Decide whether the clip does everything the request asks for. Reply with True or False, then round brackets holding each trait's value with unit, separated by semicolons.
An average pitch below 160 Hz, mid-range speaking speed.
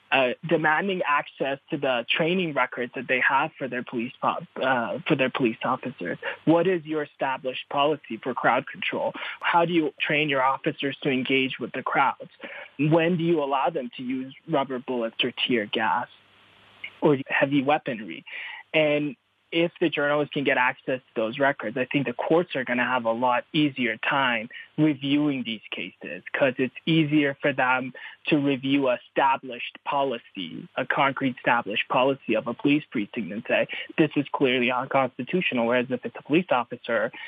True (140 Hz; 170 wpm)